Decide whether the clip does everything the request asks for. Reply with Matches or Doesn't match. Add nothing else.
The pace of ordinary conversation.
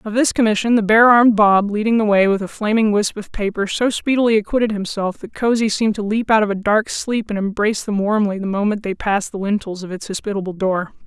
Doesn't match